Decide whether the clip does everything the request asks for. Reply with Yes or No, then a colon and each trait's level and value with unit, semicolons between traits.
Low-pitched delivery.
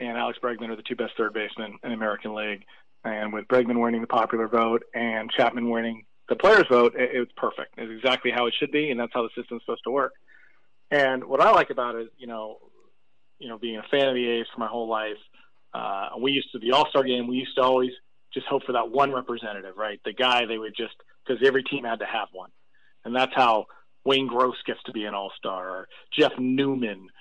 Yes: low, 120 Hz